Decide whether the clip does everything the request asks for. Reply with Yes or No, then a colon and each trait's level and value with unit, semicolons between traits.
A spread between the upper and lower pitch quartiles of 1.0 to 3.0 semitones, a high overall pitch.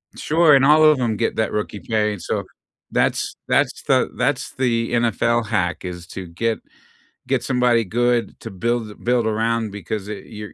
No: narrow, 2.6 semitones; low, 115 Hz